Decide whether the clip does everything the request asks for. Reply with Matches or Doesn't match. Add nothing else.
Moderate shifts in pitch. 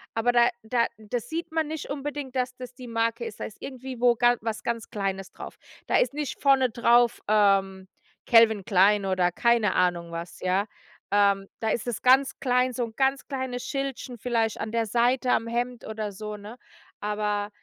Matches